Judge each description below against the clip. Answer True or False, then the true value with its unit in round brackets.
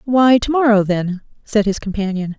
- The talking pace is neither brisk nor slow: True (175 wpm)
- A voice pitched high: True (215 Hz)